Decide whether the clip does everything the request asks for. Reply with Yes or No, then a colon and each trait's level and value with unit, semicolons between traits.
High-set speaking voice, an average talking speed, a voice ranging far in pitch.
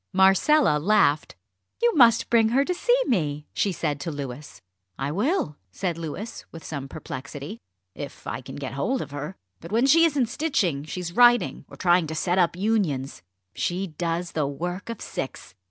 No: medium, 175 Hz; average, 175 wpm; wide, 7.7 semitones